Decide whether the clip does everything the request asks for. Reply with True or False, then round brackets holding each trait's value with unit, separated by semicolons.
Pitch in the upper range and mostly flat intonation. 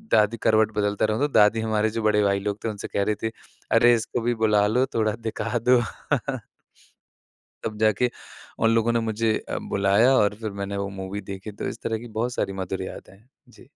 False (110 Hz; 2.0 semitones)